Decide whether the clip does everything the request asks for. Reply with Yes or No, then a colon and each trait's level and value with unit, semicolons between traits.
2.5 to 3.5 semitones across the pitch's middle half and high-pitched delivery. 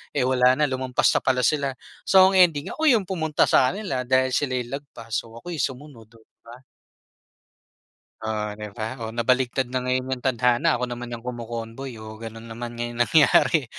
No: average, 2.8 semitones; low, 125 Hz